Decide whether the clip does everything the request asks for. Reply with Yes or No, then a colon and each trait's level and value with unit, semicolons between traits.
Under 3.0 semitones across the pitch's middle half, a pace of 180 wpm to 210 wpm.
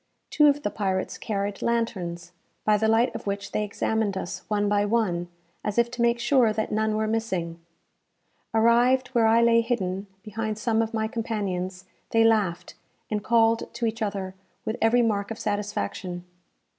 No: narrow, 2.4 semitones; average, 170 wpm